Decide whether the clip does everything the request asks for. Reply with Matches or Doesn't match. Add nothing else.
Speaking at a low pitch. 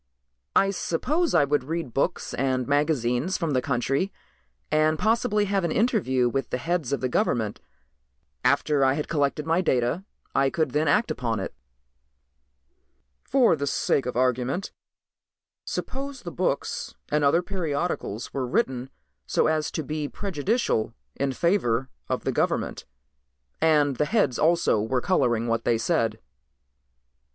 Doesn't match